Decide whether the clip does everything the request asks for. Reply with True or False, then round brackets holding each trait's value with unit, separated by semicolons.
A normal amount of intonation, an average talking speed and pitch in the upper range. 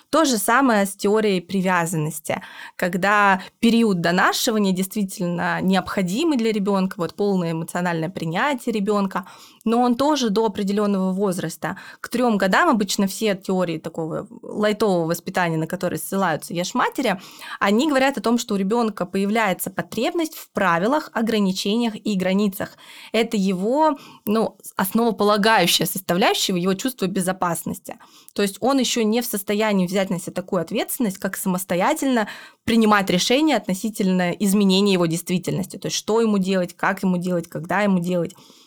True (3.7 semitones; 140 wpm; 200 Hz)